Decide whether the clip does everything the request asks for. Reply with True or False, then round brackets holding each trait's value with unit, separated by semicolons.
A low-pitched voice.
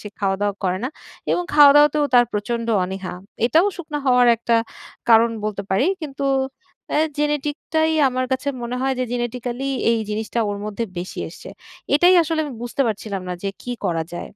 False (245 Hz)